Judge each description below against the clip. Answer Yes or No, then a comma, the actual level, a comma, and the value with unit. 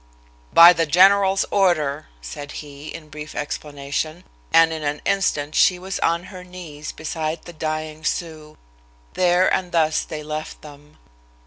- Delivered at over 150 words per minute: No, average, 145 wpm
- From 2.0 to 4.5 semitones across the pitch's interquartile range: Yes, average, 2.8 semitones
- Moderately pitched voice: Yes, medium, 155 Hz